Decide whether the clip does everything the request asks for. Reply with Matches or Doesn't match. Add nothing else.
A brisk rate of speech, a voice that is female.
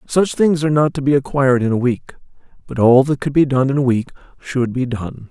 Doesn't match